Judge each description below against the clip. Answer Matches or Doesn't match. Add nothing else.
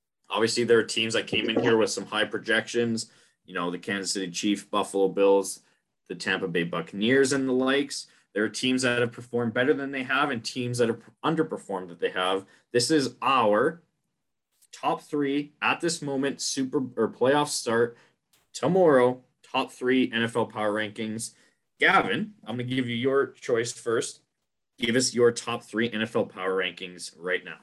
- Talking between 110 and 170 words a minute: Doesn't match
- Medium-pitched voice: Doesn't match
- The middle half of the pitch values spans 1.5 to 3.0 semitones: Doesn't match